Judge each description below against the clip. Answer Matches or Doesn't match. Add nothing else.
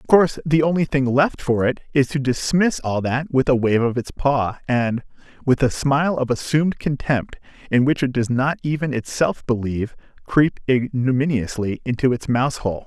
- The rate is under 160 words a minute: Doesn't match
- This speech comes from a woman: Doesn't match